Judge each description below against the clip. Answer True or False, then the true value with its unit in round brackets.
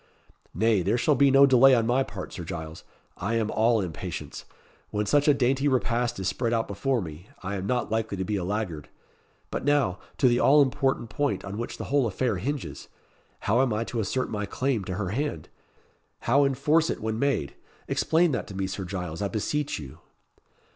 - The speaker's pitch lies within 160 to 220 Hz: False (115 Hz)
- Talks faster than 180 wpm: True (200 wpm)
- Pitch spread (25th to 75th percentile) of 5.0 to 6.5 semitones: True (5.5 semitones)